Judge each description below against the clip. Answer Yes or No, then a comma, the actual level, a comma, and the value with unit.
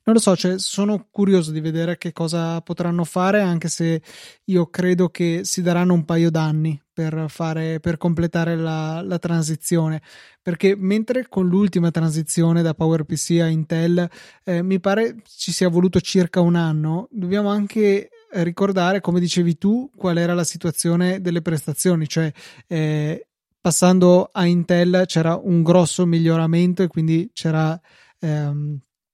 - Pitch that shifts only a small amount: Yes, narrow, 2.0 semitones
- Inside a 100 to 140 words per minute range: No, average, 150 wpm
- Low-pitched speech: No, medium, 175 Hz